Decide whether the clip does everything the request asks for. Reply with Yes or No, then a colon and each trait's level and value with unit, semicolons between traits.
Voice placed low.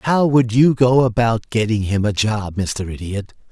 Yes: low, 115 Hz